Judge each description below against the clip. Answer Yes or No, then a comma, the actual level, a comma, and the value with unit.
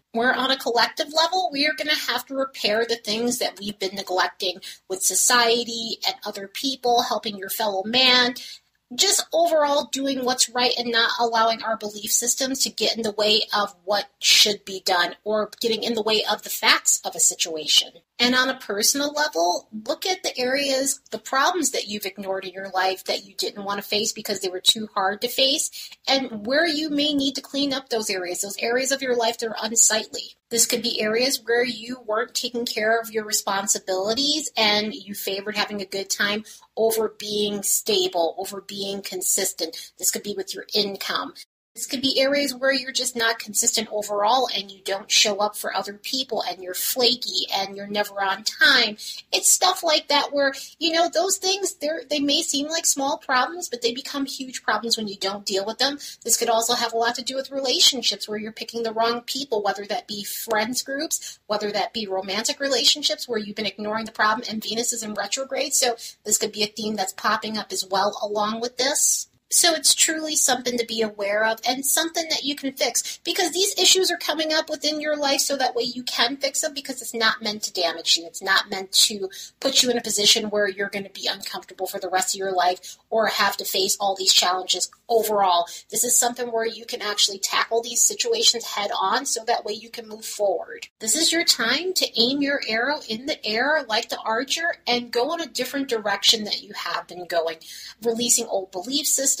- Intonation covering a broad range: No, average, 4.6 semitones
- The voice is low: No, high, 230 Hz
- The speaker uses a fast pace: Yes, fast, 215 wpm